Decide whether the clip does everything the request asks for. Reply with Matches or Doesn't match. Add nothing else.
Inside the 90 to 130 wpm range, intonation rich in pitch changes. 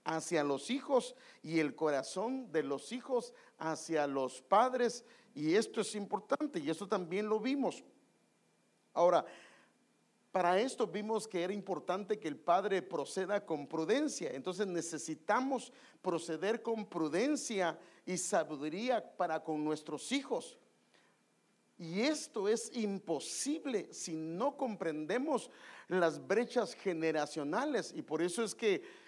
Matches